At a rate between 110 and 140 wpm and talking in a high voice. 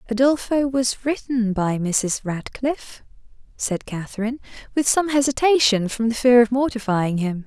Yes: slow, 135 wpm; high, 235 Hz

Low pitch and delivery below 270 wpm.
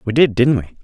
No: low, 125 Hz; fast, 285 wpm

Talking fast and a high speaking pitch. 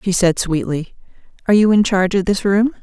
Yes: fast, 210 wpm; high, 195 Hz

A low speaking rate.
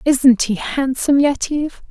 Yes: slow, 125 wpm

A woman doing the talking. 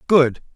No: male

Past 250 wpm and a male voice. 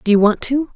No: fast, 320 wpm; female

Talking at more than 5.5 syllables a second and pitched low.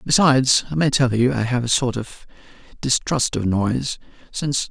No: 5.4 syllables/s; low, 125 Hz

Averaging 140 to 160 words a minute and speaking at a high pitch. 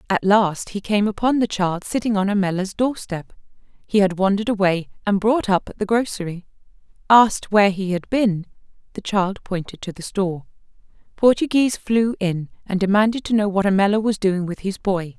No: average, 180 wpm; high, 200 Hz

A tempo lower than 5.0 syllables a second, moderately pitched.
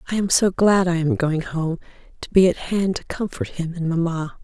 No: 5.1 syllables/s; medium, 170 Hz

